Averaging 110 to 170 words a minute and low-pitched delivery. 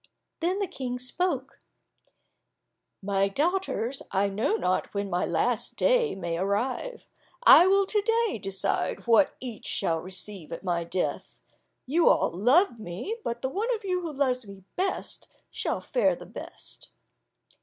No: average, 150 wpm; high, 245 Hz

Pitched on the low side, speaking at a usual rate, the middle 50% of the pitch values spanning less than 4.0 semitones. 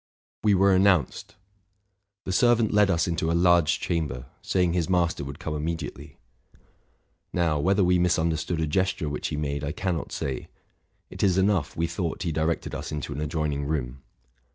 Yes: very low, 85 Hz; average, 175 wpm; average, 3.4 semitones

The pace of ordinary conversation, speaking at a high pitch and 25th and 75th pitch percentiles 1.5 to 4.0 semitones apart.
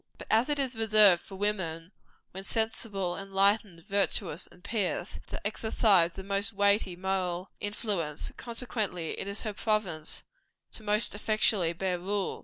Yes: average, 145 wpm; high, 200 Hz; average, 2.9 semitones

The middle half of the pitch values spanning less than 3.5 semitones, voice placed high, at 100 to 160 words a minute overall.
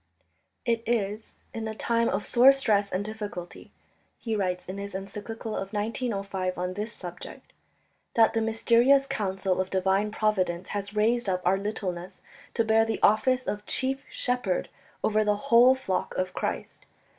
Yes: average, 3.1 semitones; high, 210 Hz; average, 155 wpm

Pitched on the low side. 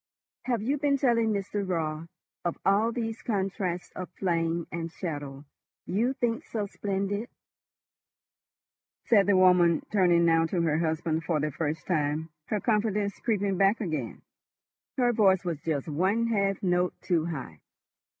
No: medium, 185 Hz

